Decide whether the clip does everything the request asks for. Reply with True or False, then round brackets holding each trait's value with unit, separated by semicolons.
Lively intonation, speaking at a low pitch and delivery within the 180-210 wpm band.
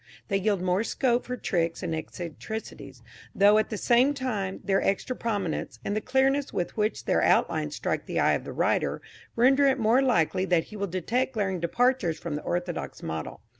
False (5.8 semitones; 210 Hz; 190 wpm)